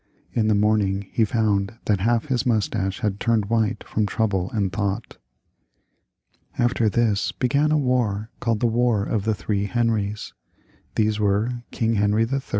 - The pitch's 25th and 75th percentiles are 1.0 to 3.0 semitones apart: Yes, narrow, 2.4 semitones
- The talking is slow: No, average, 155 wpm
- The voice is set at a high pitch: No, low, 110 Hz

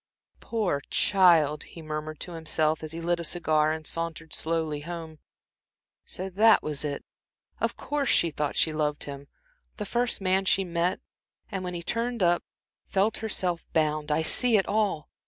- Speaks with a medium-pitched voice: Yes, medium, 165 Hz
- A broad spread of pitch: No, average, 3.8 semitones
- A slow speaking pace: No, average, 170 wpm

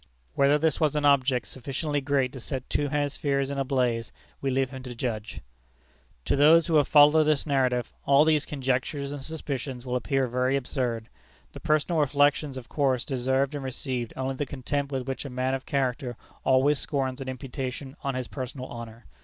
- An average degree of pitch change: No, narrow, 2.1 semitones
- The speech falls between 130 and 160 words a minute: No, average, 185 wpm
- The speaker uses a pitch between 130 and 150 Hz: Yes, low, 135 Hz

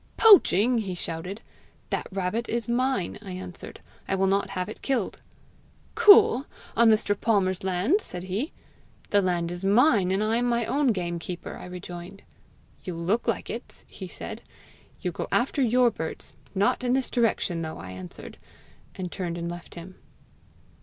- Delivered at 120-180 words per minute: Yes, average, 165 wpm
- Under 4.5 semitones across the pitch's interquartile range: No, average, 4.9 semitones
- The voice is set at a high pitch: Yes, high, 195 Hz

